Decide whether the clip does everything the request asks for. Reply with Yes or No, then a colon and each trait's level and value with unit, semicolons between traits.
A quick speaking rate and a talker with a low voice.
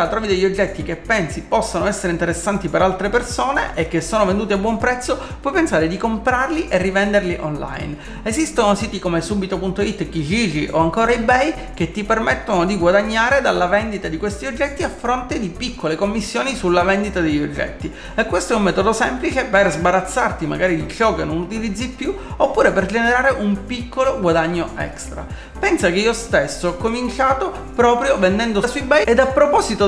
No: fast, 175 wpm; high, 205 Hz